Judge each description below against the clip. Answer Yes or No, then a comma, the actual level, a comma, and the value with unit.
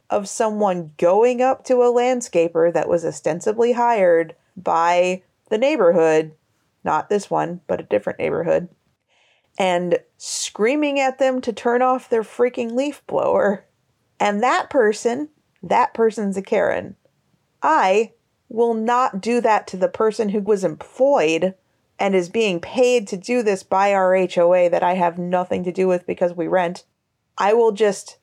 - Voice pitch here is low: No, high, 210 Hz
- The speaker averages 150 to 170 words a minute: Yes, average, 155 wpm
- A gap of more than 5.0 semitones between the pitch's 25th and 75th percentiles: Yes, wide, 5.5 semitones